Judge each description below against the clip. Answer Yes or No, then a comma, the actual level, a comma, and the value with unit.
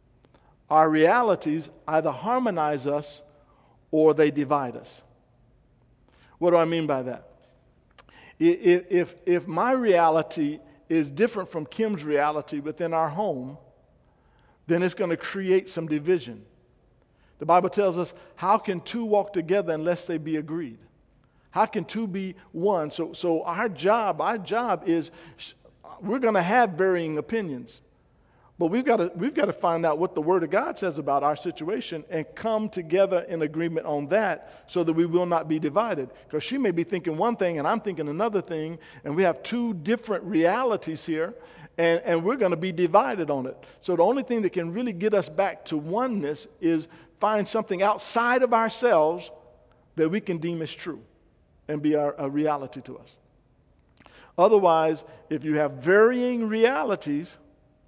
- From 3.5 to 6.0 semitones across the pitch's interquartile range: Yes, average, 4.6 semitones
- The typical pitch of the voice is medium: Yes, medium, 170 Hz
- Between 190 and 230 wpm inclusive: No, average, 170 wpm